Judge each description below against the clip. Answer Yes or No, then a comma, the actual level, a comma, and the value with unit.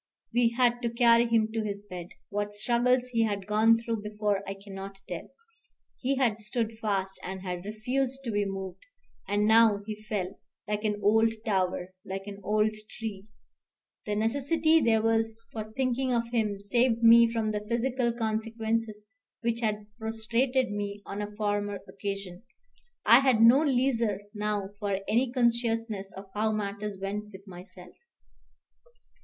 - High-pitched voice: Yes, high, 220 Hz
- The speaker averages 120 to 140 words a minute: No, average, 155 wpm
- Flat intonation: Yes, narrow, 2.3 semitones